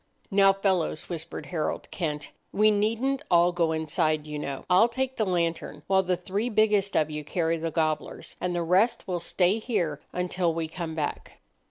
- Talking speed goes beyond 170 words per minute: Yes, average, 180 wpm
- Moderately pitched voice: Yes, medium, 175 Hz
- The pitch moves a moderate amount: Yes, average, 3.7 semitones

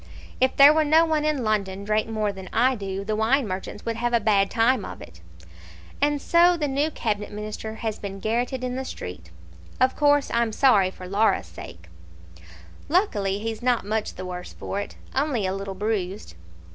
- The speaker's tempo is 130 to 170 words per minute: No, average, 195 wpm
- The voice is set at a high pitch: Yes, high, 220 Hz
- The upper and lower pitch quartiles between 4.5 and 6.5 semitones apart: Yes, average, 4.9 semitones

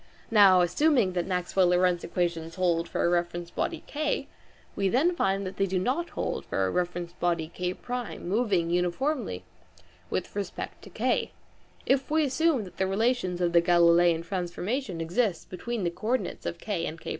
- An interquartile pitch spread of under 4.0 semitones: No, average, 5.2 semitones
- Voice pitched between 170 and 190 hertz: Yes, medium, 185 Hz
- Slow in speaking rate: No, average, 180 wpm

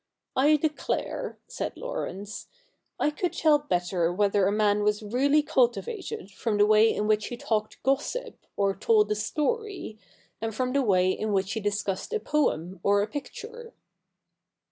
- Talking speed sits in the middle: Yes, average, 165 wpm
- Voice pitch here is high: Yes, high, 220 Hz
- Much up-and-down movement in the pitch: Yes, wide, 6.7 semitones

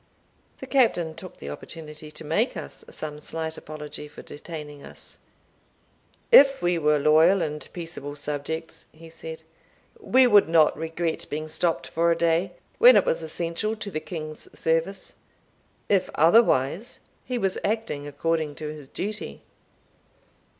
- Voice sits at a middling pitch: Yes, medium, 160 Hz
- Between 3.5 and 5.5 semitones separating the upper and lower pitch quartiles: No, average, 3.1 semitones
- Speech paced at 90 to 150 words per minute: Yes, average, 145 wpm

